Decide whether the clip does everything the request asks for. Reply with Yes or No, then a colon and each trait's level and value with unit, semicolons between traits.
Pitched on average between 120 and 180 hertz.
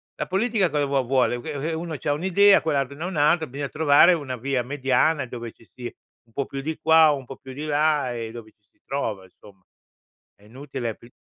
Yes: medium, 140 Hz